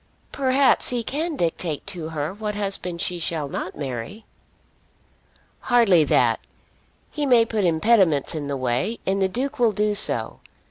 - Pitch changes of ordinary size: No, wide, 6.5 semitones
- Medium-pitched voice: No, high, 195 Hz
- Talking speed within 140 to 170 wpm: Yes, average, 150 wpm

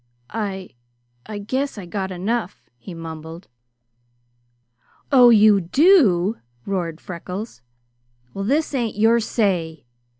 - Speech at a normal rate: No, slow, 105 wpm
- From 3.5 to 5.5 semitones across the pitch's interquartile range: Yes, average, 4.7 semitones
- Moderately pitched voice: No, high, 200 Hz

